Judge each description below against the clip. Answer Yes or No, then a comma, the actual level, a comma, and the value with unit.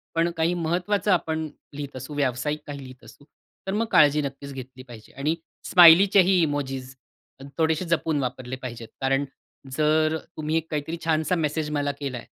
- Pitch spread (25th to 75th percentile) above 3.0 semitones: Yes, average, 3.5 semitones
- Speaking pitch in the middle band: Yes, medium, 150 Hz